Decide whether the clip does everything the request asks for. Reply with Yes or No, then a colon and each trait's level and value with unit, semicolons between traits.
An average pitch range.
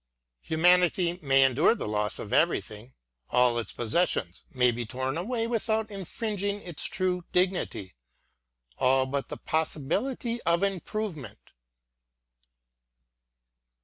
No: wide, 7.9 semitones